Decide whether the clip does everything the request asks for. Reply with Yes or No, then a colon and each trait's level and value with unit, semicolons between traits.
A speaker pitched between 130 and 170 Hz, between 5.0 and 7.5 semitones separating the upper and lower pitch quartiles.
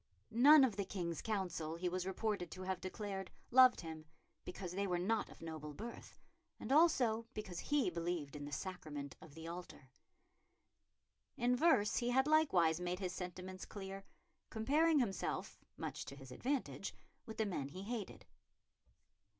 No: high, 190 Hz; average, 5.3 semitones